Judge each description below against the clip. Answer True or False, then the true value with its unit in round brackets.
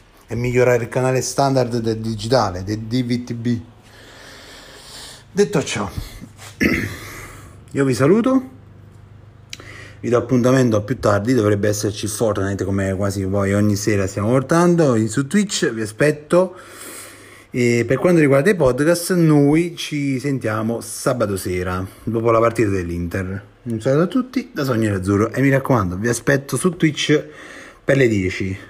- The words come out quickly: False (135 wpm)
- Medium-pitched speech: False (120 Hz)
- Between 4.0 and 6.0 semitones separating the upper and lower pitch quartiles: True (4.8 semitones)